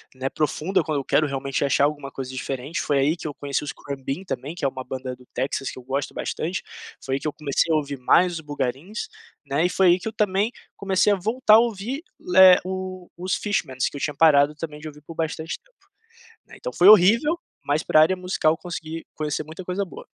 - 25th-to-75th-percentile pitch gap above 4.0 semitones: Yes, average, 4.9 semitones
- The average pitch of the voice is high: No, medium, 155 Hz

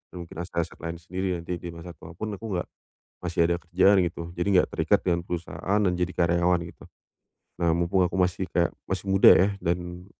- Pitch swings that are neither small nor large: No, narrow, 1.3 semitones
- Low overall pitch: Yes, very low, 90 Hz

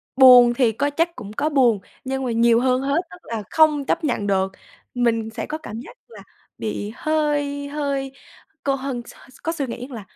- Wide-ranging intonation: No, average, 3.7 semitones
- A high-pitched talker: Yes, very high, 265 Hz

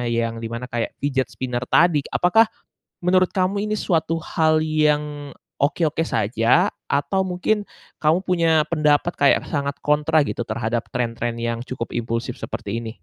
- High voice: No, medium, 145 Hz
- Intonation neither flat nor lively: No, wide, 6.3 semitones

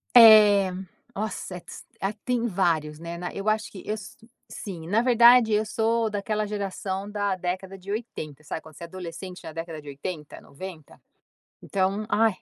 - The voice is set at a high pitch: Yes, high, 195 Hz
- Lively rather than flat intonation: No, average, 3.8 semitones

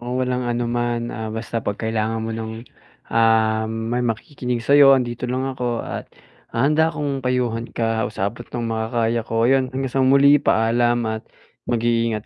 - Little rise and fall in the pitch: Yes, narrow, 2.1 semitones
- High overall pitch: No, low, 120 Hz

